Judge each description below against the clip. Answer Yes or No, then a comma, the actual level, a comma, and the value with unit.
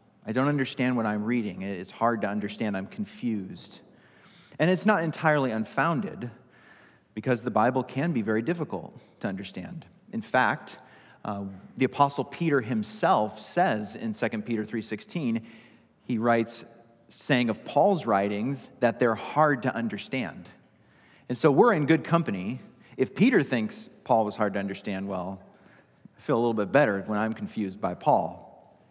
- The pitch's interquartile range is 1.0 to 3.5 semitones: No, average, 4.7 semitones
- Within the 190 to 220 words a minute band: No, average, 155 wpm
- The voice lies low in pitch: Yes, low, 115 Hz